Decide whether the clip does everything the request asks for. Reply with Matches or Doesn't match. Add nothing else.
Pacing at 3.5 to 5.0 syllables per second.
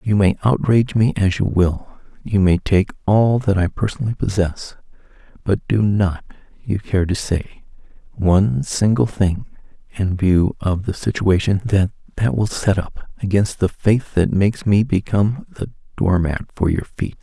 Matches